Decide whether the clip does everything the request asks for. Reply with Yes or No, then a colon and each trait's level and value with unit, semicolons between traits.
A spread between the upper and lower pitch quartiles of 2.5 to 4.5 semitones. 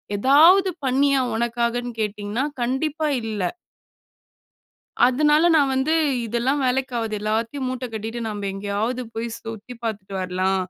Yes: average, 3.9 semitones